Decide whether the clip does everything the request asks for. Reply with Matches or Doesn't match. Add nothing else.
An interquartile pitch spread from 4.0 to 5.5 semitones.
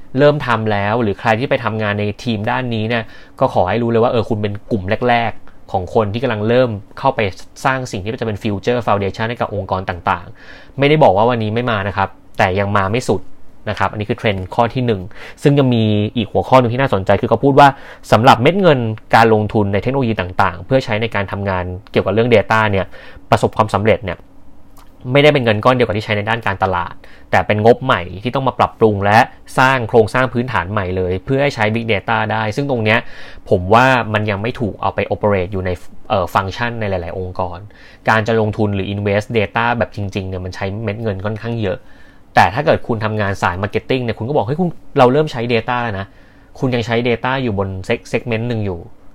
Doesn't match